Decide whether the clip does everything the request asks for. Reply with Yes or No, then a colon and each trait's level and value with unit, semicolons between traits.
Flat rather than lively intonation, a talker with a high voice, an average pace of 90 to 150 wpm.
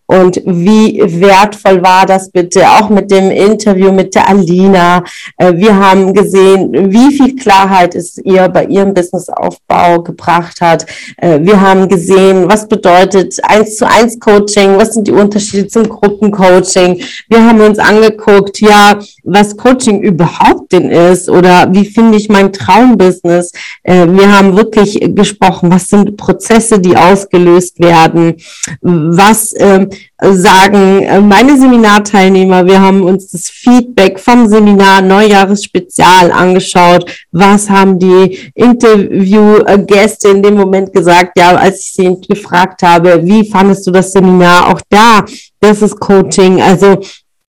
Yes: narrow, 2.2 semitones; high, 195 Hz; average, 135 wpm